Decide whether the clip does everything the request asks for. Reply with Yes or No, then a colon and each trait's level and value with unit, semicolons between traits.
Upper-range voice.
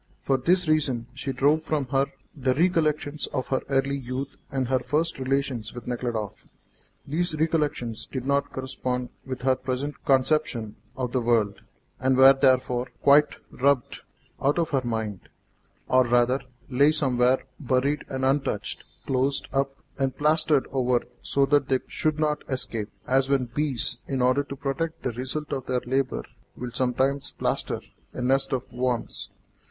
No: low, 135 Hz